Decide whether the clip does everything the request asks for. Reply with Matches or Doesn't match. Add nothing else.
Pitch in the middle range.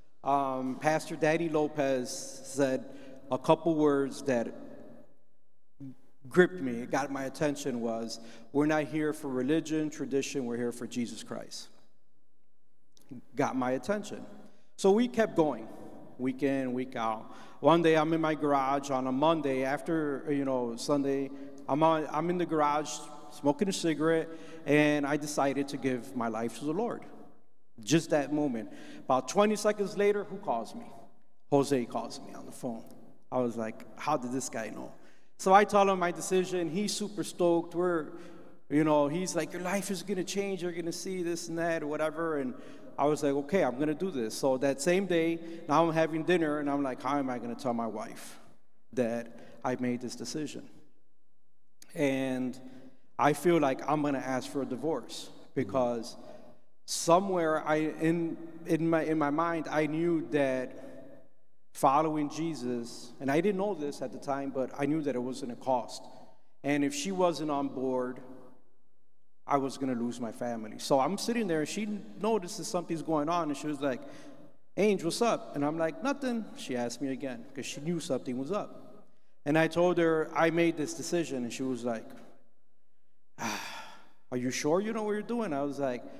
Matches